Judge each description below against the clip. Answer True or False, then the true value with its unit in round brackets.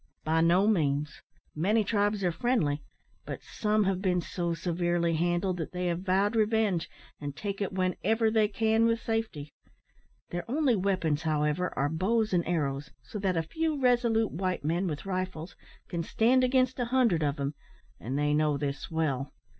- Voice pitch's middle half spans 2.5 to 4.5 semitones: False (5.5 semitones)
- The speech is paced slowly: False (170 wpm)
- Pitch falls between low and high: True (180 Hz)